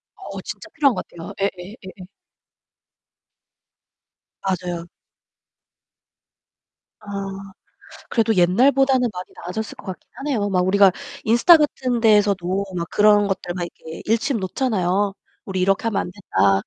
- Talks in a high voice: Yes, high, 200 Hz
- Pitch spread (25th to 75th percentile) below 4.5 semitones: Yes, average, 3.9 semitones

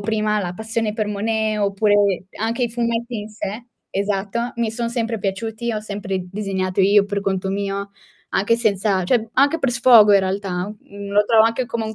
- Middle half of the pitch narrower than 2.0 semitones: No, narrow, 2.4 semitones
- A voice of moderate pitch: No, high, 210 Hz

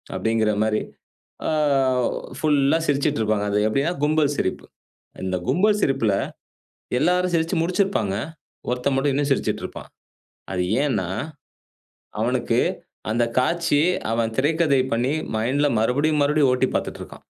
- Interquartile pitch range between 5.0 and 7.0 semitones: Yes, wide, 5.4 semitones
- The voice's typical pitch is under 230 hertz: Yes, medium, 140 Hz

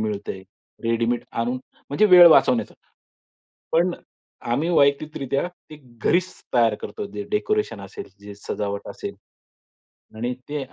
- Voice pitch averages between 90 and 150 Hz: Yes, low, 135 Hz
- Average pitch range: No, wide, 7.5 semitones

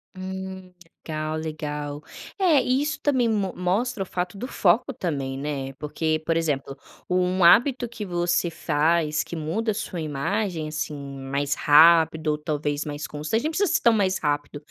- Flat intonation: No, average, 4.8 semitones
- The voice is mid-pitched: Yes, medium, 170 Hz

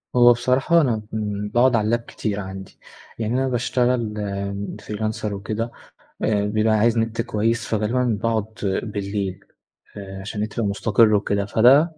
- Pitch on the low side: Yes, low, 110 Hz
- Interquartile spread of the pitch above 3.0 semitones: No, narrow, 2.5 semitones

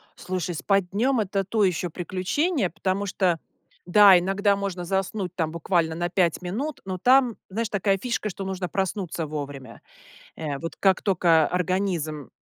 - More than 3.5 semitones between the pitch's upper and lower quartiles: No, average, 2.7 semitones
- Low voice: No, medium, 185 Hz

